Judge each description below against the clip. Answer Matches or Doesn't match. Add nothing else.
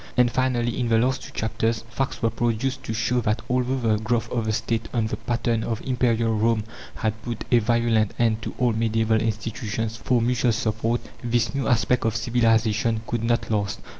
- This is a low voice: Matches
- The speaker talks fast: Doesn't match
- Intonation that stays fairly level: Matches